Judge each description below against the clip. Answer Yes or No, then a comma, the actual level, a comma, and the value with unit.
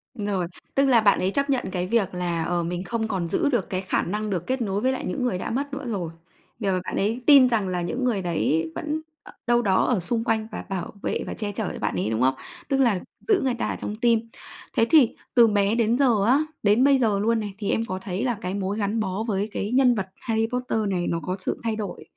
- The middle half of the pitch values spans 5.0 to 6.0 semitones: No, average, 4.5 semitones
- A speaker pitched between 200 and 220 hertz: Yes, high, 215 Hz